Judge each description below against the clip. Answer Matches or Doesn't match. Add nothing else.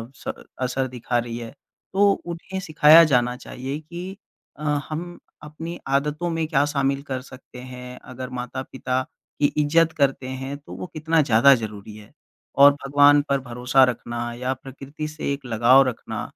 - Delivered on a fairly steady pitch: Doesn't match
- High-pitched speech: Doesn't match